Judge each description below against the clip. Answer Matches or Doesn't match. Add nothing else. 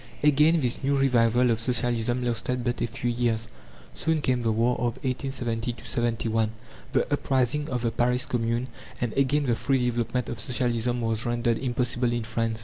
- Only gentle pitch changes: Matches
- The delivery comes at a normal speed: Matches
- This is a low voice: Matches